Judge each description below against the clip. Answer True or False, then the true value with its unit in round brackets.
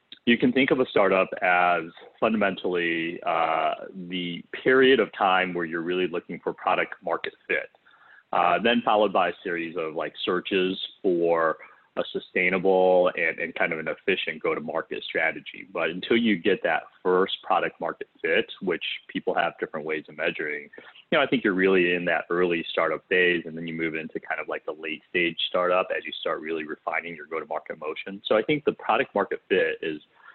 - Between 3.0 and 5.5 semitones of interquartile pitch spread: False (2.5 semitones)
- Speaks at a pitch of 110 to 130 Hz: False (90 Hz)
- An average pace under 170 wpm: False (190 wpm)